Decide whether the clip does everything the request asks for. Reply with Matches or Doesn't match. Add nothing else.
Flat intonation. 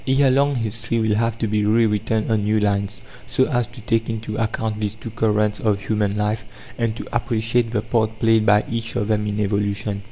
Matches